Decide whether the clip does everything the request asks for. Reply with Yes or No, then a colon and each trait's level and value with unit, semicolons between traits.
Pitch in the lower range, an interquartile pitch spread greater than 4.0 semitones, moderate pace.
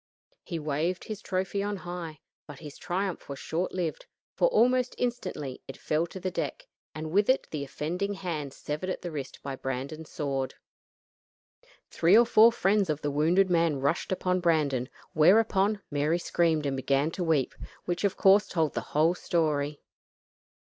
No: medium, 170 Hz; average, 4.4 semitones; average, 170 wpm